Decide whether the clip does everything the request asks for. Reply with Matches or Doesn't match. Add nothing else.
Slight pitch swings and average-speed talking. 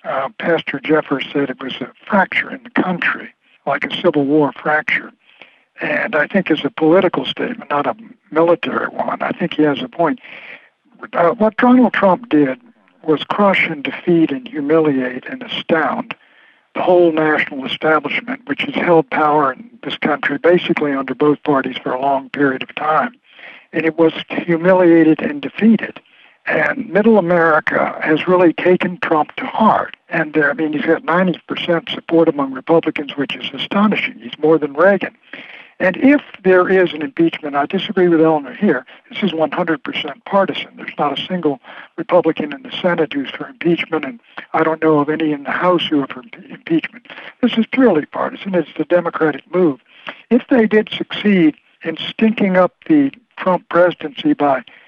Doesn't match